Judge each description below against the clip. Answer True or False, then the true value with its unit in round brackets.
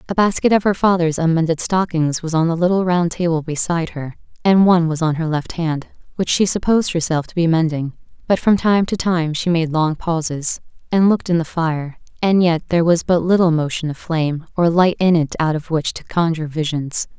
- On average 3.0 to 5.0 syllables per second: False (5.5 syllables/s)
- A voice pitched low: False (170 Hz)